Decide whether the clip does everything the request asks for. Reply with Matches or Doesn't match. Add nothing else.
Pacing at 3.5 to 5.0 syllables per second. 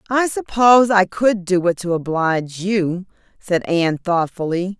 Matches